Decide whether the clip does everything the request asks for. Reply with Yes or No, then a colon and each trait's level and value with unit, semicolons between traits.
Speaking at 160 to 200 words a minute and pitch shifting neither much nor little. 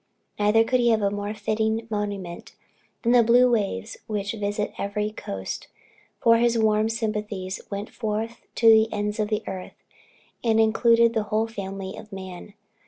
No: average, 165 wpm; narrow, 1.8 semitones